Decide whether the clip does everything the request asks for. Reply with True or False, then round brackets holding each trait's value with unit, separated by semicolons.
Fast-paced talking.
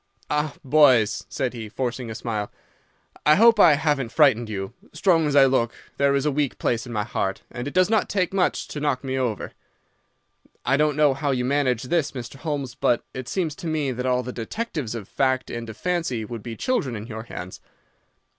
True (210 wpm)